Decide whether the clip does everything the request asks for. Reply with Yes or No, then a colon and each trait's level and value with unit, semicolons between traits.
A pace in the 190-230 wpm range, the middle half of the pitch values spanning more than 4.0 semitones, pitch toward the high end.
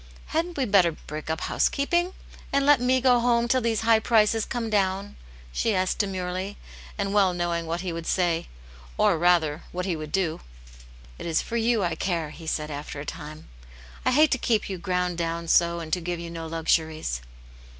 No: fast, 205 wpm; wide, 5.5 semitones; medium, 180 Hz